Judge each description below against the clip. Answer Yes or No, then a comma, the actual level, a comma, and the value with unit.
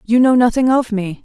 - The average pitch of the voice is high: Yes, high, 235 Hz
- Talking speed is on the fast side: Yes, fast, 240 wpm